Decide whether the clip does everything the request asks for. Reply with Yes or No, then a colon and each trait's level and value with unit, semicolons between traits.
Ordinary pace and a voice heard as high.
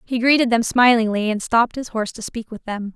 No: fast, 245 wpm; high, 230 Hz